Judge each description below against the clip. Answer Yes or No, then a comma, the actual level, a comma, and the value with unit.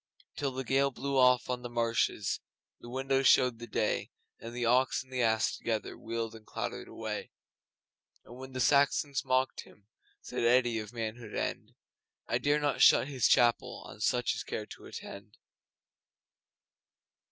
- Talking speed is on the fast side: No, average, 165 wpm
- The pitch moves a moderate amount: No, narrow, 2.3 semitones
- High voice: No, low, 125 Hz